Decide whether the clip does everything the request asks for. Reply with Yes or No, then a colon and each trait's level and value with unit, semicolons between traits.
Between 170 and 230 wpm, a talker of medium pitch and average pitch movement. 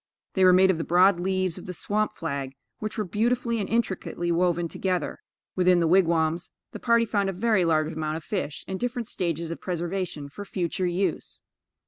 Yes: average, 190 wpm; medium, 180 Hz; average, 3.0 semitones